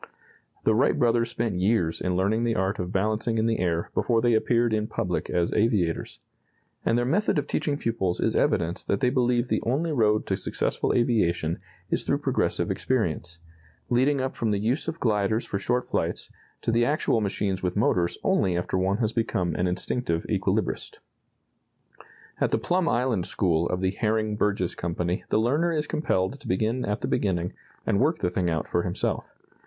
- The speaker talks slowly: No, average, 185 wpm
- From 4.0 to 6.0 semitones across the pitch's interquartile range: Yes, average, 4.7 semitones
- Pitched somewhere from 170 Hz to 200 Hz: No, low, 110 Hz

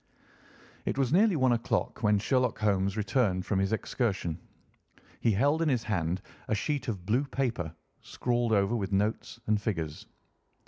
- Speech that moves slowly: No, average, 155 wpm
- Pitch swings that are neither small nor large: Yes, average, 4.5 semitones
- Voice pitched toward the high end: No, low, 110 Hz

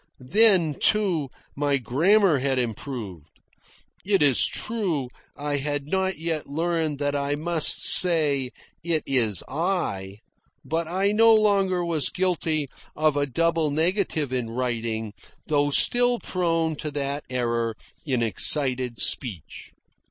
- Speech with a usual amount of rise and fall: Yes, average, 5.0 semitones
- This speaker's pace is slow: Yes, slow, 125 wpm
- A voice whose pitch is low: No, medium, 150 Hz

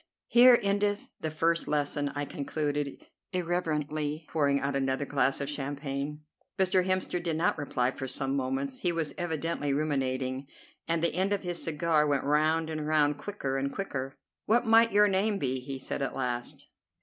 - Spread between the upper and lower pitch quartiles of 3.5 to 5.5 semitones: Yes, average, 3.8 semitones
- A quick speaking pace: No, average, 170 wpm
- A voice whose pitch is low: No, medium, 150 Hz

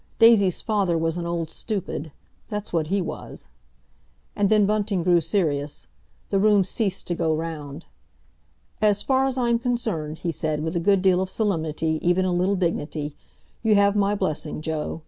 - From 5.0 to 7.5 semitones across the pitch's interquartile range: No, average, 4.3 semitones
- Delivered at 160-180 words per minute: Yes, average, 165 wpm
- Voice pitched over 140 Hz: Yes, medium, 185 Hz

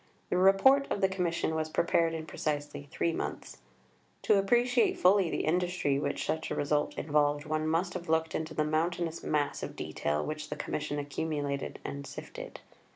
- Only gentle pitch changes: No, average, 3.3 semitones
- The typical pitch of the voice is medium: Yes, medium, 160 Hz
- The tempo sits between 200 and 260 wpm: No, average, 170 wpm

